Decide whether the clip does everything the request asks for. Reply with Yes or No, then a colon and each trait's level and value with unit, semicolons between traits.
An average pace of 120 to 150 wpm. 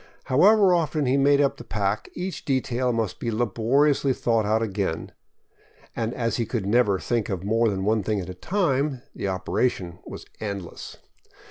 No: average, 170 wpm